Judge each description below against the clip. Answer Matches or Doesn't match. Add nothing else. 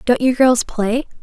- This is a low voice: Doesn't match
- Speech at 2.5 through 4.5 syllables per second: Matches